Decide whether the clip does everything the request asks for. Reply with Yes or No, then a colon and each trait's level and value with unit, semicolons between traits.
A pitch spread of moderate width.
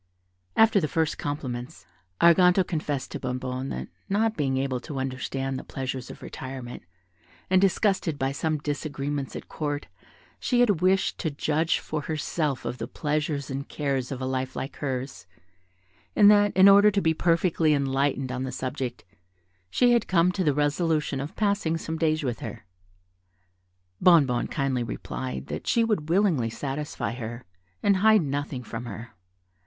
Yes: average, 4.4 semitones